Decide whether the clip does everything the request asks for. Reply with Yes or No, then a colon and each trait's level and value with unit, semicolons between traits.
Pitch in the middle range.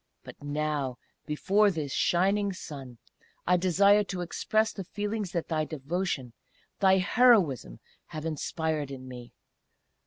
Yes: medium, 170 Hz